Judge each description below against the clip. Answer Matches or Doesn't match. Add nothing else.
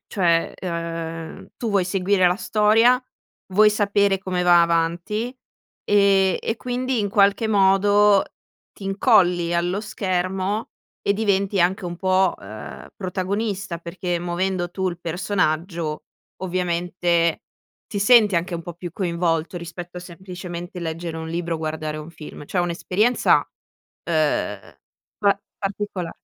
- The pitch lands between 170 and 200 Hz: Matches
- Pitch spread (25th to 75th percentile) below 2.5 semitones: Doesn't match